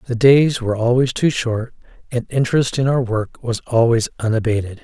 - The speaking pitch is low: Yes, low, 120 Hz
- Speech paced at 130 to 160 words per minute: No, average, 175 wpm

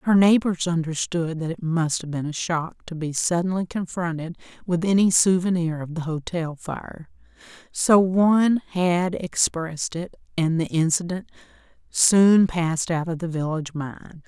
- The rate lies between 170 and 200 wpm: No, average, 145 wpm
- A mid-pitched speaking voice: Yes, medium, 170 Hz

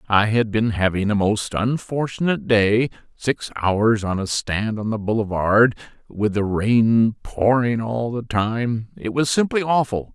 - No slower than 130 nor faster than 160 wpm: Yes, average, 155 wpm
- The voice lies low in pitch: Yes, low, 110 Hz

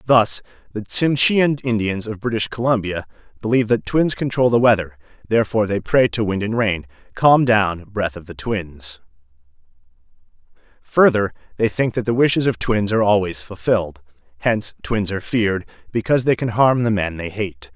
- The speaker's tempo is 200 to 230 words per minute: No, average, 165 wpm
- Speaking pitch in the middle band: No, low, 105 Hz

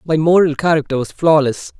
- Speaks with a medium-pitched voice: Yes, medium, 155 Hz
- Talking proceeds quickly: No, average, 165 wpm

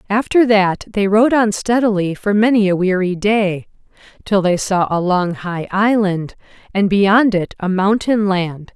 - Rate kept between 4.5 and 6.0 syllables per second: No, 4.3 syllables/s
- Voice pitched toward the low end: No, high, 200 Hz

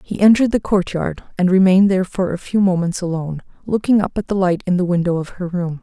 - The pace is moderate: No, fast, 235 wpm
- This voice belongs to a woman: Yes, female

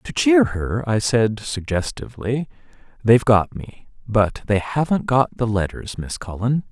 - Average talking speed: Yes, average, 150 wpm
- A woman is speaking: No, male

